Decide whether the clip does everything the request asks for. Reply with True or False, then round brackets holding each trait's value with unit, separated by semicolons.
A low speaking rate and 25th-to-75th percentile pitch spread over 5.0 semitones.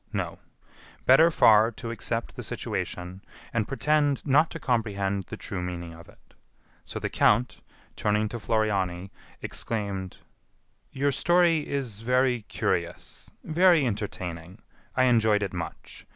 True (130 wpm; 5.5 semitones)